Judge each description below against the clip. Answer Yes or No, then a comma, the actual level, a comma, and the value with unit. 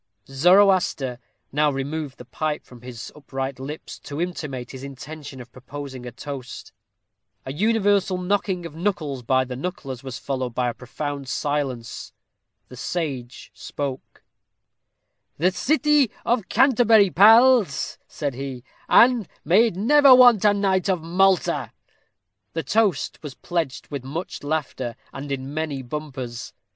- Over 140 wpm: No, slow, 135 wpm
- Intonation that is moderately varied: No, wide, 6.3 semitones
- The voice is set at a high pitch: No, medium, 150 Hz